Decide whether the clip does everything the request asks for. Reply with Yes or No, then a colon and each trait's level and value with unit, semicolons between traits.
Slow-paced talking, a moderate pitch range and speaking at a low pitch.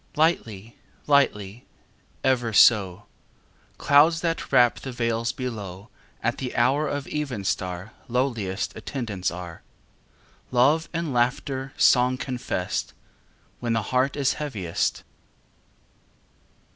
Yes: slow, 100 wpm; average, 4.8 semitones; low, 120 Hz